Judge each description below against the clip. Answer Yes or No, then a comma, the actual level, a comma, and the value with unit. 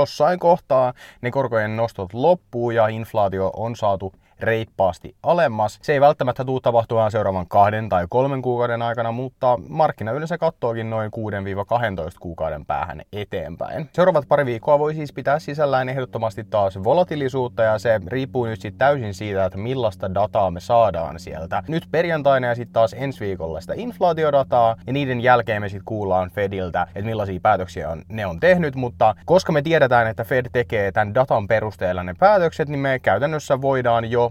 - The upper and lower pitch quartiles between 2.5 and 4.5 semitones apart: No, average, 5.0 semitones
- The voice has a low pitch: Yes, low, 115 Hz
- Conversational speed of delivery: No, fast, 165 wpm